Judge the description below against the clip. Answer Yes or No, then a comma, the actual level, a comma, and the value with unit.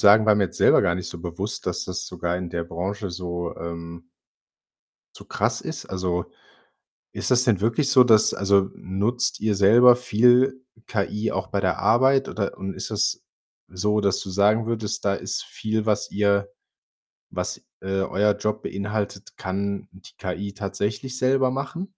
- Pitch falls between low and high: No, low, 100 Hz